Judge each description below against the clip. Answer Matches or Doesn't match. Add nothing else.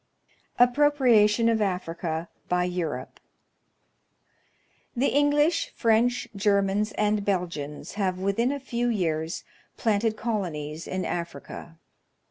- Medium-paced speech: Doesn't match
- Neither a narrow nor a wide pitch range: Matches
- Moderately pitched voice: Doesn't match